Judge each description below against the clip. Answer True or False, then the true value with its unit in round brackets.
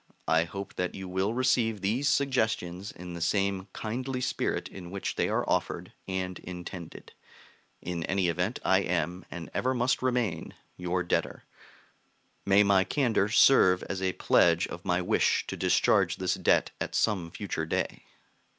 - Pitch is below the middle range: True (95 Hz)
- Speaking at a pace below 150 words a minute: False (160 wpm)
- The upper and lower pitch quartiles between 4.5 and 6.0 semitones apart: False (3.9 semitones)